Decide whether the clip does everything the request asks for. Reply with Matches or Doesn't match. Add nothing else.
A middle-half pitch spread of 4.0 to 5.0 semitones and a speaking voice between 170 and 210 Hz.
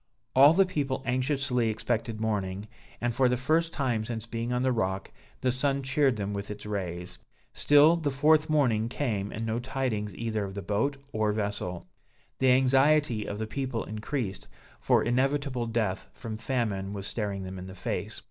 Doesn't match